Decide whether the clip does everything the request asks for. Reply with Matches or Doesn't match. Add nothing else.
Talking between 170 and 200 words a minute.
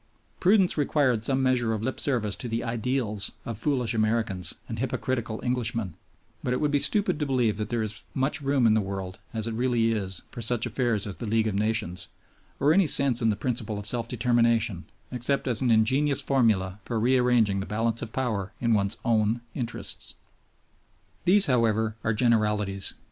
Matches